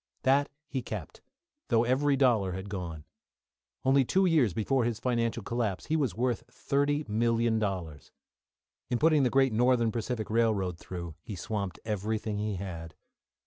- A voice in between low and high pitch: No, low, 115 Hz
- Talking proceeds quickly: No, average, 145 wpm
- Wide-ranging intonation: No, average, 4.6 semitones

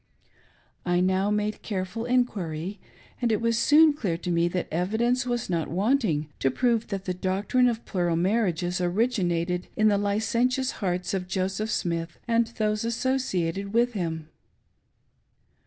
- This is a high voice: Yes, high, 200 Hz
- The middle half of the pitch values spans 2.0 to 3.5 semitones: No, average, 4.6 semitones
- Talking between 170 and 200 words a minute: No, average, 155 wpm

